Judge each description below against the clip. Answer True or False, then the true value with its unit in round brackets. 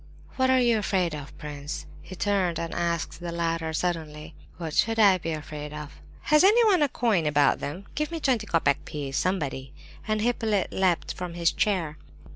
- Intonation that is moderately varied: False (5.9 semitones)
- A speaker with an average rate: True (185 wpm)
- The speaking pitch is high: False (175 Hz)